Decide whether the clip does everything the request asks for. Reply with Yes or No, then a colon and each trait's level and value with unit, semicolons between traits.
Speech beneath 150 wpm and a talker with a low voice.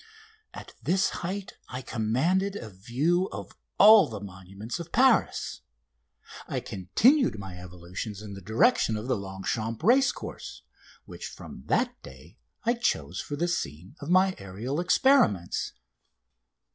Yes: slow, 135 wpm; low, 120 Hz